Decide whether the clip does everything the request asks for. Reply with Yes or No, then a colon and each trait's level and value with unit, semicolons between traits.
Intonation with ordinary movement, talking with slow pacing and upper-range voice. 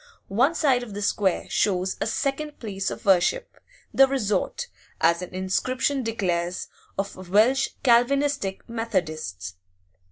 No: wide, 6.1 semitones; slow, 125 wpm; high, 210 Hz